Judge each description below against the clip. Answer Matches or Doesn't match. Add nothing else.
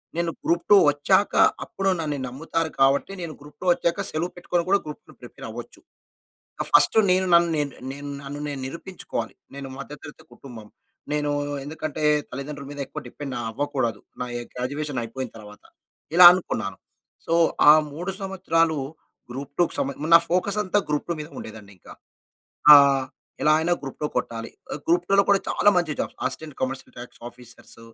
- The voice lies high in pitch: Doesn't match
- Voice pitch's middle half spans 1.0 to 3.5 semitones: Doesn't match